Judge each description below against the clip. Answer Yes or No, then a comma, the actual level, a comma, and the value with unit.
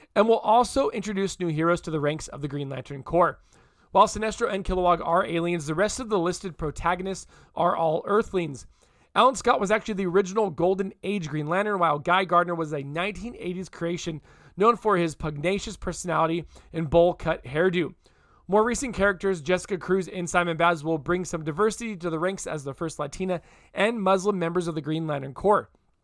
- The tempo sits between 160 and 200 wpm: Yes, average, 185 wpm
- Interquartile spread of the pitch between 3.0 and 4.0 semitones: Yes, average, 3.5 semitones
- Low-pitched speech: No, medium, 175 Hz